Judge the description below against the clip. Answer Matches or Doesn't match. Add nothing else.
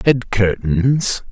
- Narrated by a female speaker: Doesn't match